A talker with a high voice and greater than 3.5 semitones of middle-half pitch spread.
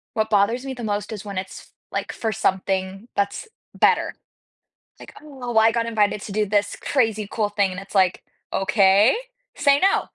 No: high, 210 Hz; average, 2.7 semitones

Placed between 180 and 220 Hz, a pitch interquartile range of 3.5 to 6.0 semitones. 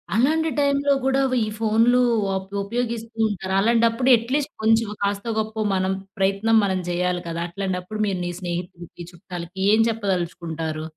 Yes: high, 200 Hz; average, 4.1 semitones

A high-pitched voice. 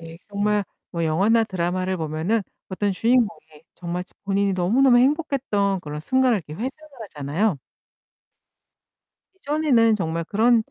Yes: high, 200 Hz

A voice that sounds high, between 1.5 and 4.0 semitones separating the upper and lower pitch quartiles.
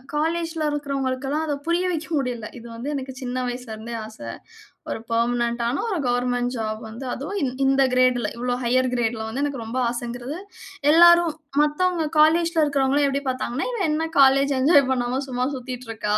Yes: very high, 260 Hz; average, 3.4 semitones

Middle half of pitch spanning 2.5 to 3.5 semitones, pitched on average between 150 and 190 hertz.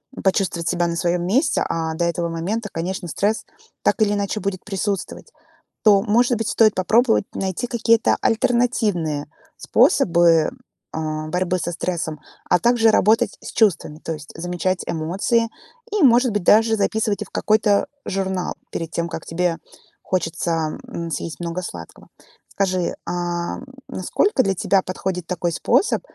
No: average, 4.3 semitones; medium, 185 Hz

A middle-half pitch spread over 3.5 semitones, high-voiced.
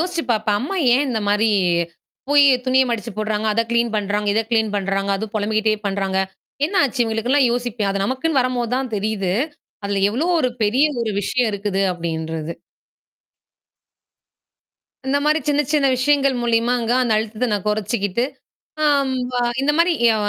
Yes: average, 4.0 semitones; high, 225 Hz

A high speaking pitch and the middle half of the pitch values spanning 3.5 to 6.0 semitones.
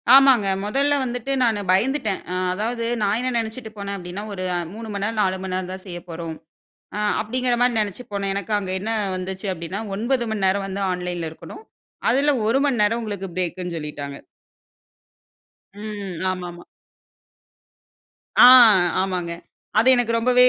Yes: high, 200 Hz; average, 4.0 semitones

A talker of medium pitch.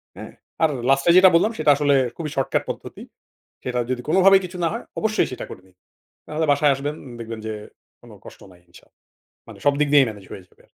Yes: medium, 145 Hz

